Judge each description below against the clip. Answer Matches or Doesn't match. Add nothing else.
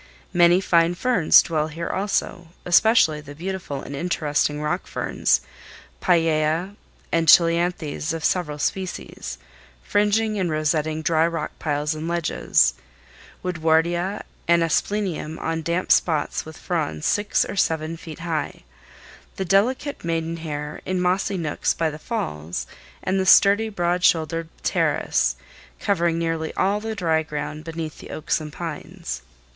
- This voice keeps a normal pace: Doesn't match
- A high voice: Doesn't match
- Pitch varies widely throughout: Doesn't match